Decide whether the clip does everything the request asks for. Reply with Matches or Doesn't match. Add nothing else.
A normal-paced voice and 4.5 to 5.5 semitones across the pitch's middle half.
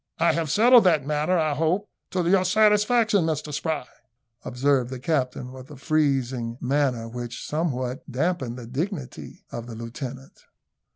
Matches